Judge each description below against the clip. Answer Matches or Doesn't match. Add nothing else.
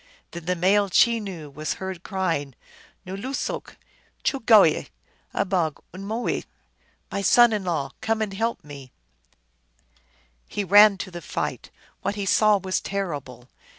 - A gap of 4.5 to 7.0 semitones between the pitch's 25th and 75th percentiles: Matches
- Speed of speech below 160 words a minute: Matches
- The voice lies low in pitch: Doesn't match